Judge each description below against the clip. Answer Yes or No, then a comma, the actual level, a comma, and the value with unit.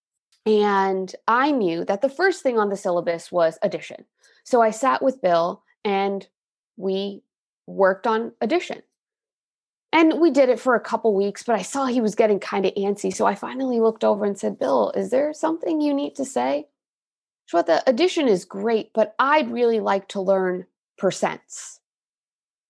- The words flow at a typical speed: Yes, average, 175 wpm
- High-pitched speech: Yes, high, 220 Hz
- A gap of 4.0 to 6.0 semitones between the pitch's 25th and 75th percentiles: Yes, wide, 5.4 semitones